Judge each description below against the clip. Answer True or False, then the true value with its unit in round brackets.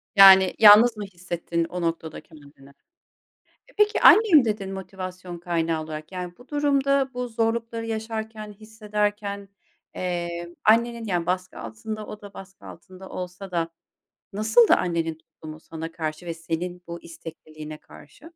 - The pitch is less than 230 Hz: True (185 Hz)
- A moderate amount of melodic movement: True (4.5 semitones)